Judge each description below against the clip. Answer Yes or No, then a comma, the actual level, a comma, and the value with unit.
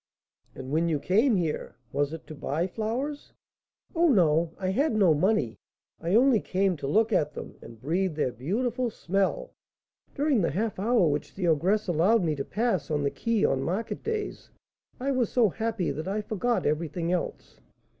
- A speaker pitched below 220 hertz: Yes, high, 190 Hz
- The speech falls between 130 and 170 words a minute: No, average, 180 wpm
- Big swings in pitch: Yes, wide, 6.3 semitones